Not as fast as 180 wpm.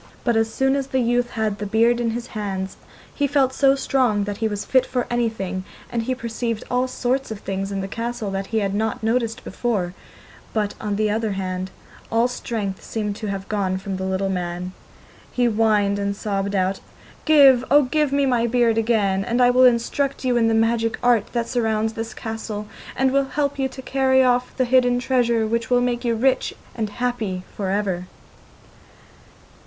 No: average, 200 wpm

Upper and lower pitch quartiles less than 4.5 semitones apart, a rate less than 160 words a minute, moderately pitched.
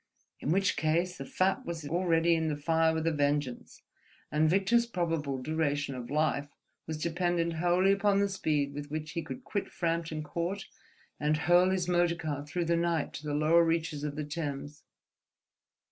No: average, 2.8 semitones; average, 175 wpm; medium, 165 Hz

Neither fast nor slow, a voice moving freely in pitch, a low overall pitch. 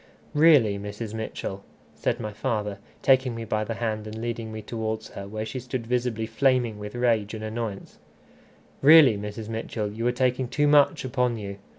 No: average, 180 wpm; narrow, 2.6 semitones; low, 115 Hz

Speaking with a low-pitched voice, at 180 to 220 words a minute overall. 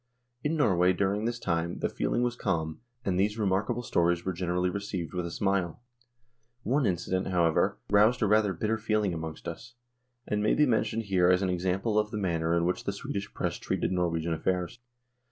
Yes: very low, 95 Hz; average, 190 wpm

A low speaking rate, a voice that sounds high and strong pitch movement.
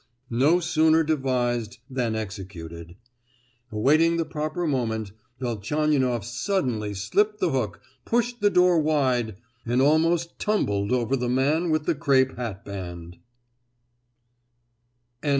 No: slow, 110 wpm; low, 130 Hz; wide, 6.3 semitones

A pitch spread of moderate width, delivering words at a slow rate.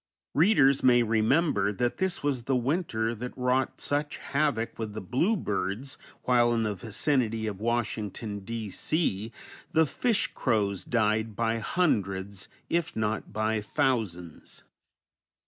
Yes: average, 4.2 semitones; slow, 130 wpm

